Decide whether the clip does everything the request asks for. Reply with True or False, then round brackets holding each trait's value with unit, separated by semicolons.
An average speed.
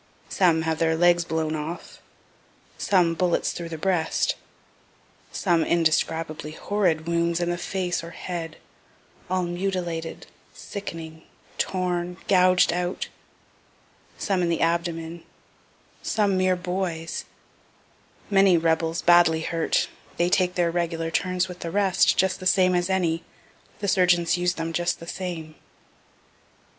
False (130 wpm)